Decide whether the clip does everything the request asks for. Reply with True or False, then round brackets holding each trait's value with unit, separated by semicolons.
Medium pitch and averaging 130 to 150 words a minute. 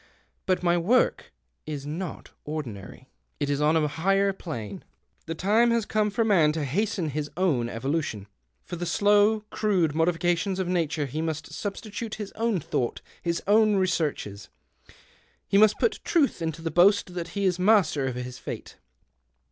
False (175 Hz; 165 wpm)